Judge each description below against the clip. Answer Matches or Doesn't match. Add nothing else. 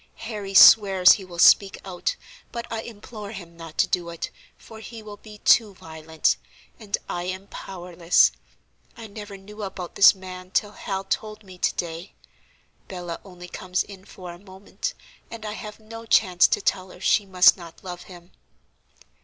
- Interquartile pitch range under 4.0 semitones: Matches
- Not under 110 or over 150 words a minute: Doesn't match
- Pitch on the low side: Doesn't match